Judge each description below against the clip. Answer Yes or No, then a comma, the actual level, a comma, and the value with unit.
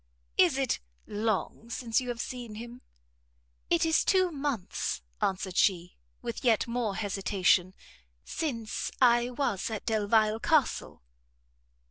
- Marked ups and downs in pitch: No, average, 3.5 semitones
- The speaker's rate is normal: No, slow, 120 wpm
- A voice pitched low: No, high, 225 Hz